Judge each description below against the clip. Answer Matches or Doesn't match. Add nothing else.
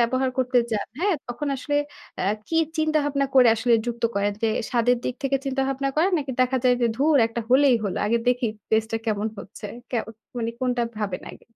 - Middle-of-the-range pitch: Doesn't match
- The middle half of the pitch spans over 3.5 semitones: Doesn't match